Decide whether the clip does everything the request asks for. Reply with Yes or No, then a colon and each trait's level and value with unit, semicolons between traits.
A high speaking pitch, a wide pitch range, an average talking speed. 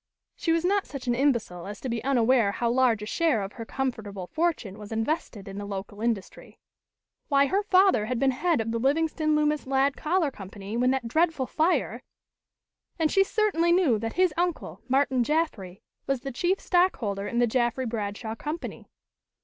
Yes: very high, 260 Hz; wide, 6.4 semitones; average, 180 wpm